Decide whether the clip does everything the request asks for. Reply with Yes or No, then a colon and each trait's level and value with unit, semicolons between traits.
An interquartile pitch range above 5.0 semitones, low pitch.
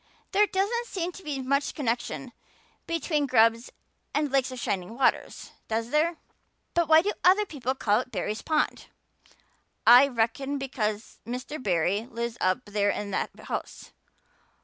No: wide, 5.4 semitones; very high, 260 Hz